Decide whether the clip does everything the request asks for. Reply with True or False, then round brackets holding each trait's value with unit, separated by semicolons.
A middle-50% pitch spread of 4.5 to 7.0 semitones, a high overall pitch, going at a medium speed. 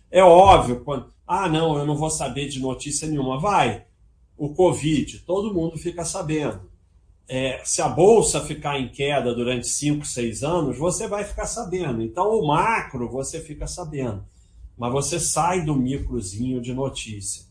False (5.2 semitones; 145 Hz; 160 wpm)